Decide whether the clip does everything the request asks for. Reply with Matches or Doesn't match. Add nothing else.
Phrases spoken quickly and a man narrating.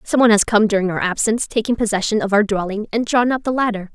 Doesn't match